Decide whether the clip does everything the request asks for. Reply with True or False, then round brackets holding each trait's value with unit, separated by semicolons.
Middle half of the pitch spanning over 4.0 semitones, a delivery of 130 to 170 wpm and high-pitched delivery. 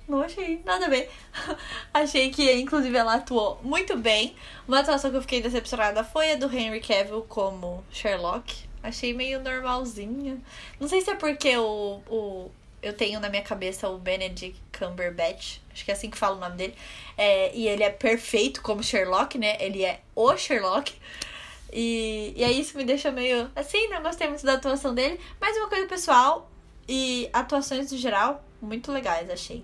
False (5.0 semitones; 180 wpm; 245 Hz)